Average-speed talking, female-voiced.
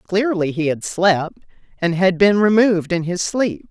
Yes: average, 180 wpm; female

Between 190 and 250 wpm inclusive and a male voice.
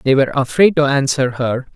Yes: fast, 205 wpm; male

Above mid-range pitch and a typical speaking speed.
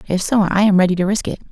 No: high, 195 Hz; fast, 320 wpm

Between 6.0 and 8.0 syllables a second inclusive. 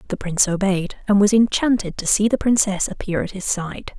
No: 5.5 syllables/s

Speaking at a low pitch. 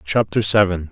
Yes: very low, 95 Hz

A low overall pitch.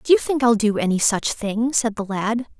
No: high, 225 Hz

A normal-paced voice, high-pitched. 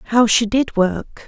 Yes: average, 190 wpm; high, 225 Hz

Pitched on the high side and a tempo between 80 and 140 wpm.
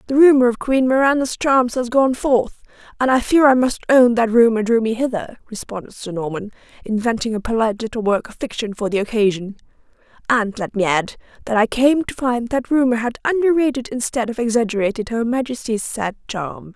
No: high, 235 Hz; average, 195 wpm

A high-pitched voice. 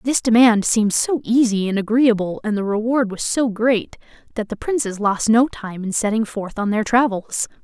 Yes: high, 220 Hz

